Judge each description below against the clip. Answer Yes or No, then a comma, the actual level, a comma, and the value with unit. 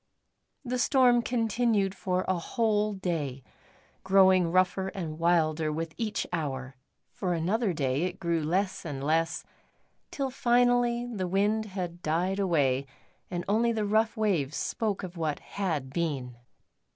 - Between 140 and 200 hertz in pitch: Yes, medium, 185 Hz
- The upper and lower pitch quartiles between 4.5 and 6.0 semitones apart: Yes, average, 5.1 semitones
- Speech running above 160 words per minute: No, average, 140 wpm